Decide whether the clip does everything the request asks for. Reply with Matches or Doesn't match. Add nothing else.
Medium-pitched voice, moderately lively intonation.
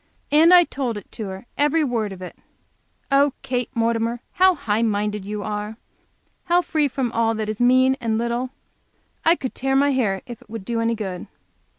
Doesn't match